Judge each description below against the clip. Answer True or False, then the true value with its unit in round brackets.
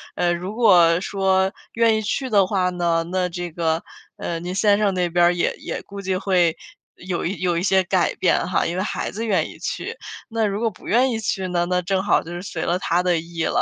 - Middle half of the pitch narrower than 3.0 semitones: True (2.5 semitones)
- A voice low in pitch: False (185 Hz)